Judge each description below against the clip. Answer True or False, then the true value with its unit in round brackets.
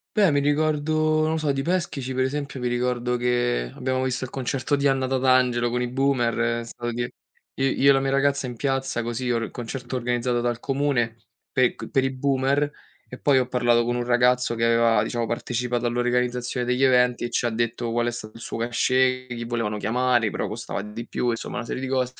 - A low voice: True (125 Hz)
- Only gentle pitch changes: True (1.9 semitones)